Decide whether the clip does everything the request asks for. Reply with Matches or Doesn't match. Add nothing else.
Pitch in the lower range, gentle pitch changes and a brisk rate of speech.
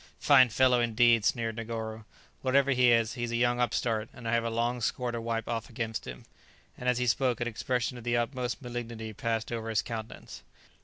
Matches